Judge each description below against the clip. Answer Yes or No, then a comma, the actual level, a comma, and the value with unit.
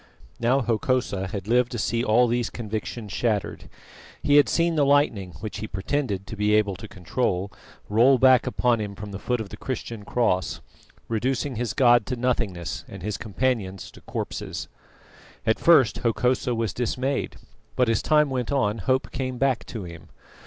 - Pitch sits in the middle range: No, low, 115 Hz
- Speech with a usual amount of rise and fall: Yes, average, 3.8 semitones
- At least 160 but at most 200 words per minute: Yes, average, 175 wpm